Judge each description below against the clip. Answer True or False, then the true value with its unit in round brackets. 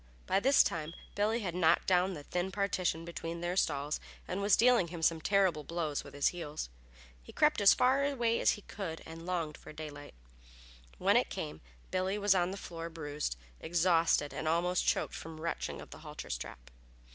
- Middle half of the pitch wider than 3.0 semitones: True (3.5 semitones)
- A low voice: False (170 Hz)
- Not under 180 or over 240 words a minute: True (195 wpm)